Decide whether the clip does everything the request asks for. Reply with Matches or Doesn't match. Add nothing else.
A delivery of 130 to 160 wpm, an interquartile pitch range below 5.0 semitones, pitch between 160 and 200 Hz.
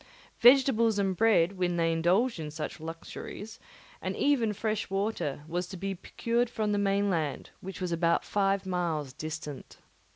Matches